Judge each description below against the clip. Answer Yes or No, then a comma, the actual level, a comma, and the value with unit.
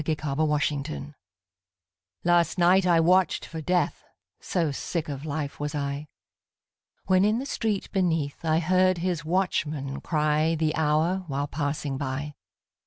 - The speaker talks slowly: No, average, 150 wpm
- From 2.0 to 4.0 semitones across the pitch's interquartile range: Yes, average, 3.3 semitones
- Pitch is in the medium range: Yes, medium, 155 Hz